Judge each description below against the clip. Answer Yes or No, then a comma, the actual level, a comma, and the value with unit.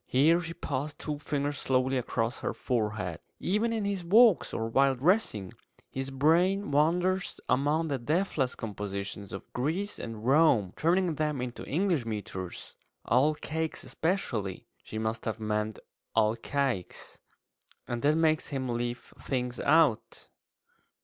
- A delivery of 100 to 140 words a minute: Yes, slow, 135 wpm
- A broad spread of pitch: Yes, wide, 6.2 semitones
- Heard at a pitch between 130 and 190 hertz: Yes, low, 135 Hz